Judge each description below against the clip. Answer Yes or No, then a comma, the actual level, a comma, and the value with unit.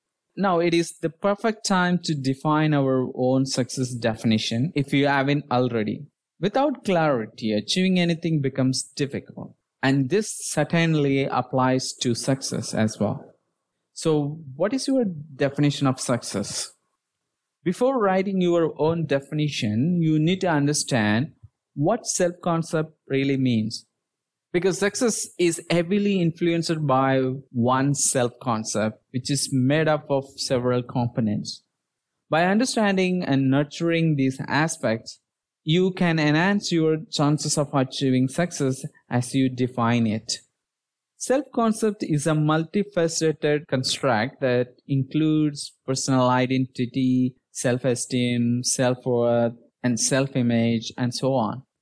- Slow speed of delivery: Yes, slow, 120 wpm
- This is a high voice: No, medium, 140 Hz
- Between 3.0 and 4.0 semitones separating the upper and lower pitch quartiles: No, average, 4.8 semitones